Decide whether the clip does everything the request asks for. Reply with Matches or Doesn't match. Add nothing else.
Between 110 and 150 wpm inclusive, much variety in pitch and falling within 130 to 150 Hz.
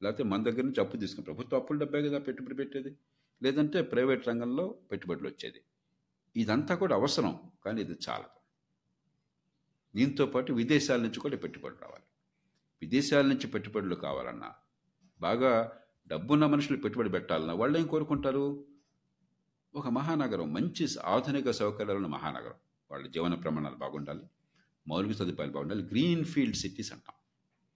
Matches